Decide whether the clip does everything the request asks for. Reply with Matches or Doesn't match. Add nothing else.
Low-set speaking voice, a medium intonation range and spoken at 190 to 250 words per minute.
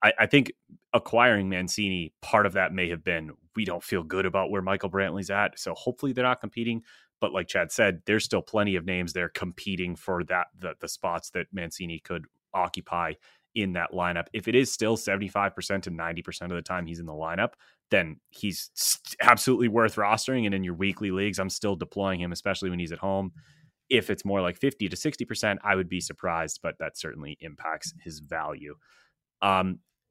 Matches